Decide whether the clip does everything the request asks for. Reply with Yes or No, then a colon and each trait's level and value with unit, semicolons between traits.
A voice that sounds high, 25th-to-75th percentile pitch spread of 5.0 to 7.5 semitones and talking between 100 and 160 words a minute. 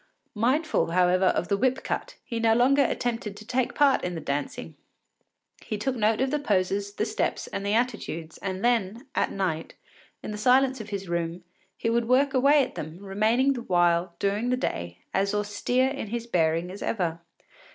No: high, 210 Hz; wide, 5.4 semitones; average, 190 wpm